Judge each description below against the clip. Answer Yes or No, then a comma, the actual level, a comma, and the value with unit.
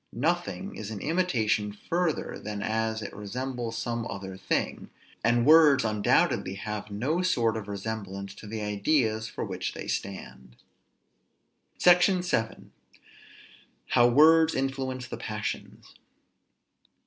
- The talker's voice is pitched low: Yes, low, 110 Hz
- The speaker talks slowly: Yes, slow, 120 wpm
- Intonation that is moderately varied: Yes, average, 4.9 semitones